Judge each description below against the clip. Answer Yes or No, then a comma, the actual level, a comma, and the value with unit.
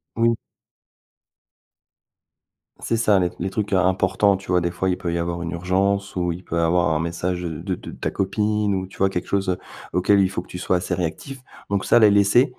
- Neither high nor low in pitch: No, very low, 95 Hz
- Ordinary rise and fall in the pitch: No, narrow, 2.2 semitones